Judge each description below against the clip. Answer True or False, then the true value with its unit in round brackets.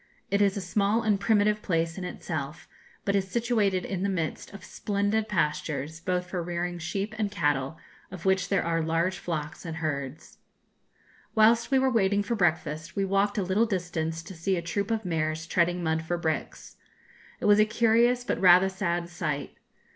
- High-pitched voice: False (180 Hz)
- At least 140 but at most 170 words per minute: False (185 wpm)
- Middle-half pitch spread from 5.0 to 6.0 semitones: False (3.7 semitones)